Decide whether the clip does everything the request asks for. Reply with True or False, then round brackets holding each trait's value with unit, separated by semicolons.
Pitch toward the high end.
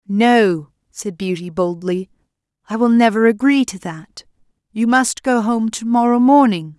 True (210 Hz)